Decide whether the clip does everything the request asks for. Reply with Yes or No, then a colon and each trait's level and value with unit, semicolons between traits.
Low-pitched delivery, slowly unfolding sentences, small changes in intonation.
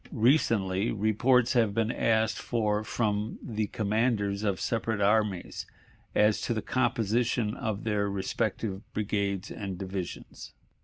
Yes: low, 105 Hz; slow, 120 wpm; narrow, 2.2 semitones